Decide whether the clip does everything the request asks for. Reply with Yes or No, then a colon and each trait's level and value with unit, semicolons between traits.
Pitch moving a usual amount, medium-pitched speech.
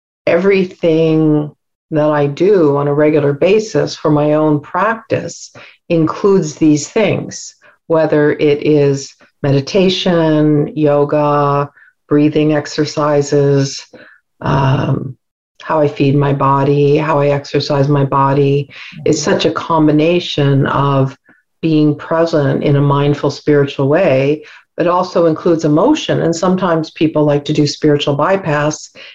No: narrow, 2.0 semitones; medium, 150 Hz